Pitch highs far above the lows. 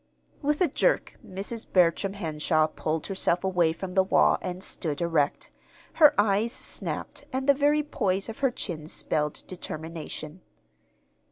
Yes: wide, 6.3 semitones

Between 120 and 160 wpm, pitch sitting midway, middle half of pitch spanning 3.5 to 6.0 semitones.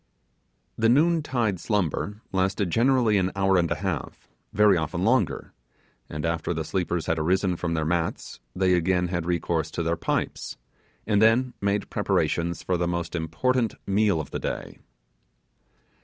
No: average, 155 wpm; very low, 95 Hz; average, 3.8 semitones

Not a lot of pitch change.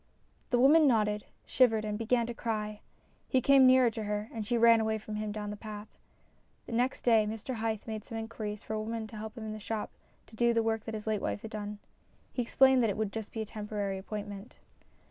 Yes: narrow, 1.6 semitones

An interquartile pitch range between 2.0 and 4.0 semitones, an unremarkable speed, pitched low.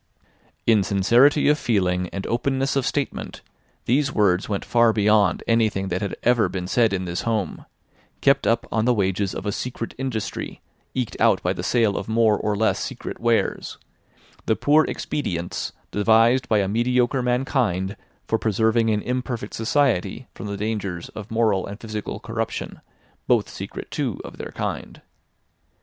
Yes: average, 3.3 semitones; average, 160 wpm; low, 110 Hz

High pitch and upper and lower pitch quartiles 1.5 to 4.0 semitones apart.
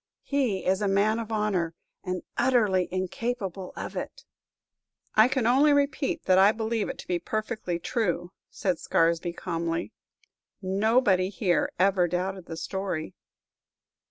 Yes: high, 195 Hz; average, 3.7 semitones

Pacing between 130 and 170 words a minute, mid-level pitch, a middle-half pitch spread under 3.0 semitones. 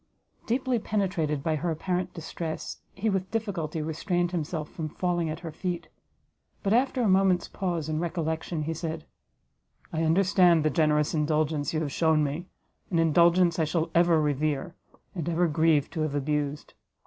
Yes: average, 160 wpm; medium, 165 Hz; narrow, 2.5 semitones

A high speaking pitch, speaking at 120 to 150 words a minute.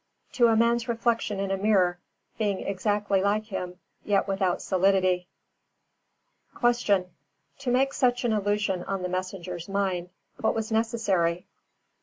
Yes: high, 200 Hz; average, 140 wpm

